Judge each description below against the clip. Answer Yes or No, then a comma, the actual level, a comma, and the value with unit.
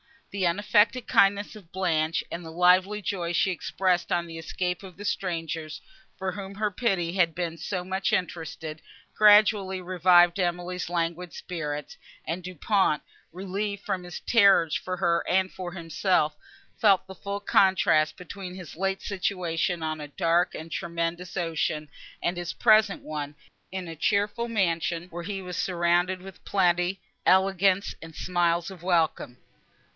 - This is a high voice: No, medium, 180 Hz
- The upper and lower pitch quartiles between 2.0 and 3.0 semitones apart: Yes, narrow, 2.4 semitones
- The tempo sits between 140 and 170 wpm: Yes, average, 150 wpm